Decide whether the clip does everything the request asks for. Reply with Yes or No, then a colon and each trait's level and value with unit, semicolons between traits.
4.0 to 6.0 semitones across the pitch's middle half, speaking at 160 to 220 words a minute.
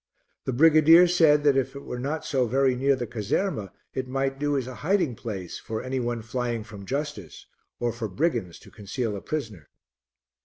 Yes: average, 4.5 semitones; average, 190 wpm